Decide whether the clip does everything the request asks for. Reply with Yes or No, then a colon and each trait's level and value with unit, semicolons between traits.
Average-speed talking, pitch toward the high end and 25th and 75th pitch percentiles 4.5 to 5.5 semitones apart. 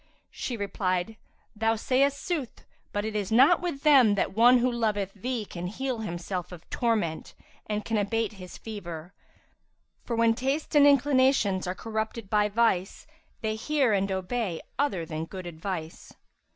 Yes: average, 155 wpm; high, 220 Hz; average, 4.8 semitones